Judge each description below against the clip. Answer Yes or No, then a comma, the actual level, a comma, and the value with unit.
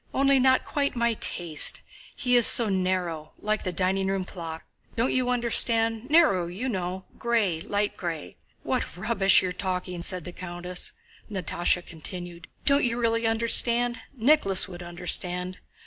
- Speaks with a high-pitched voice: Yes, high, 195 Hz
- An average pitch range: Yes, average, 4.8 semitones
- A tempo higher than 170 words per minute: No, average, 140 wpm